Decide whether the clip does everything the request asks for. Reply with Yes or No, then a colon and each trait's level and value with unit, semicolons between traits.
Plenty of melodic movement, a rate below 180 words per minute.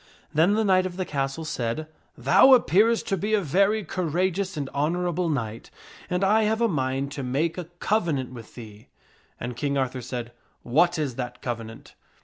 No: wide, 6.5 semitones; average, 190 wpm